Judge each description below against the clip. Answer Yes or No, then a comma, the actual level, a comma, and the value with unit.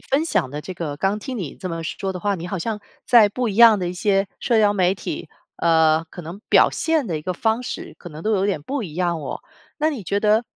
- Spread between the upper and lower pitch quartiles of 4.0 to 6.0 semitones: Yes, average, 4.5 semitones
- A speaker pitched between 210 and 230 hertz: No, high, 195 Hz